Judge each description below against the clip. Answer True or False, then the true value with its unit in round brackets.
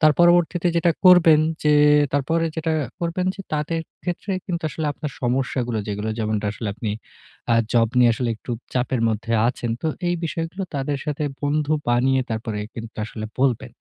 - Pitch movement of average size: False (5.7 semitones)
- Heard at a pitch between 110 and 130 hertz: False (140 Hz)